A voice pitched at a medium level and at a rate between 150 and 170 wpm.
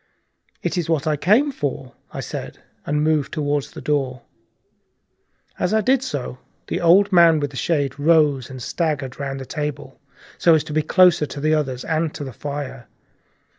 No: medium, 150 Hz; average, 180 wpm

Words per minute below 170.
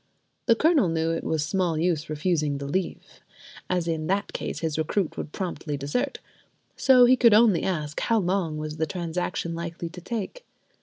No: average, 175 wpm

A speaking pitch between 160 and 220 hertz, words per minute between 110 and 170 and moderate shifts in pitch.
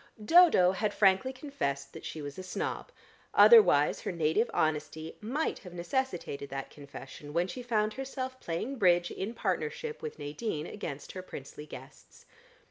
No: medium, 185 Hz; average, 150 wpm; wide, 9.0 semitones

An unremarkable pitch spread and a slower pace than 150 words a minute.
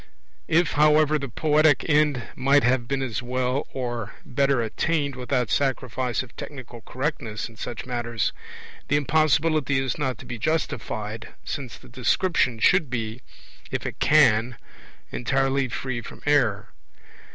Yes: average, 3.5 semitones; average, 140 wpm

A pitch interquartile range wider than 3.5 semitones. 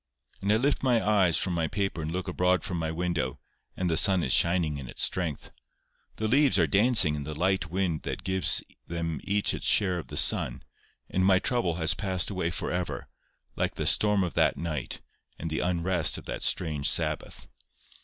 No: average, 3.1 semitones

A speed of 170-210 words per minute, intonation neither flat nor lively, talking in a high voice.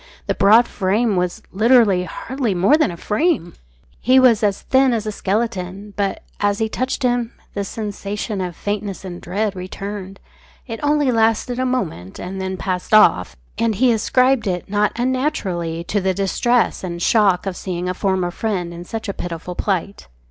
Yes: average, 175 wpm; average, 4.0 semitones; high, 205 Hz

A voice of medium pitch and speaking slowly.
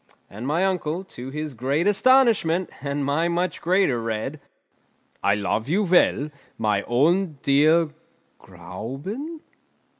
Yes: medium, 155 Hz; slow, 120 wpm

